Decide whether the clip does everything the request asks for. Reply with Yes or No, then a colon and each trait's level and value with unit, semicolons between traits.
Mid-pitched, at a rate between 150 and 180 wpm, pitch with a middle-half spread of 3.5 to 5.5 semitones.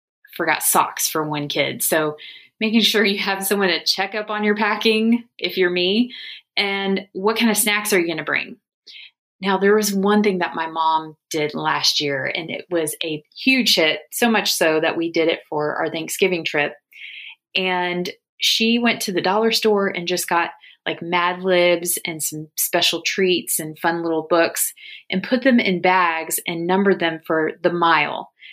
No: medium, 180 Hz; average, 190 wpm; average, 4.4 semitones